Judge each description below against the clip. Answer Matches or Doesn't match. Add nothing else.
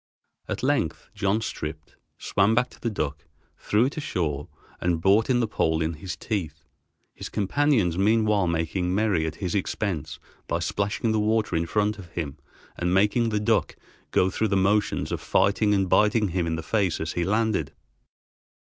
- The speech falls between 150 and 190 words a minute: Matches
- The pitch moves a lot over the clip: Doesn't match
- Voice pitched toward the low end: Matches